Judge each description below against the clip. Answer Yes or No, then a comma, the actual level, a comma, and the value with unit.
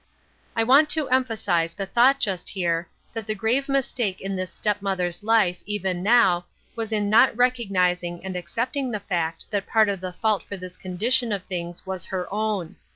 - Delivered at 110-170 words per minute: No, average, 185 wpm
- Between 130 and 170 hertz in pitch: No, high, 200 Hz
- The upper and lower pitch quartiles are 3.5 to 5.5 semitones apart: Yes, average, 4.0 semitones